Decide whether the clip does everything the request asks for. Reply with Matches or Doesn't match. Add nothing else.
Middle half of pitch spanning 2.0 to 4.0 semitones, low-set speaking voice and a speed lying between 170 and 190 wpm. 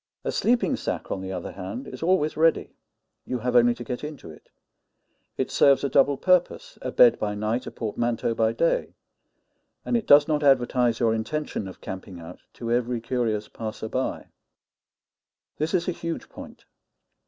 Doesn't match